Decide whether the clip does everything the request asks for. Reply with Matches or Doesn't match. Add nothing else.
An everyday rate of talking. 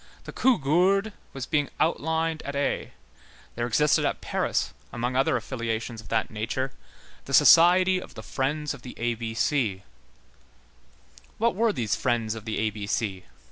Matches